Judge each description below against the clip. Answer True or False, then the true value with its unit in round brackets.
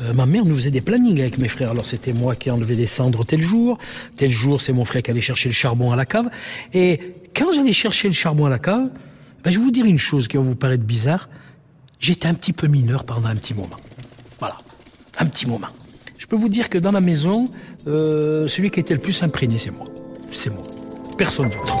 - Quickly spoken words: True (240 wpm)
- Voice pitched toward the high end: False (140 Hz)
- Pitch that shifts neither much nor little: False (6.7 semitones)